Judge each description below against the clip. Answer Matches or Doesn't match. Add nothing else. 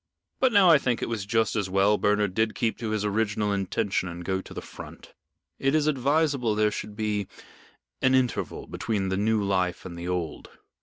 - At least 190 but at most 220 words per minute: Matches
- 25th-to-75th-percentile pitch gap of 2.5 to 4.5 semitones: Matches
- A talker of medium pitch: Doesn't match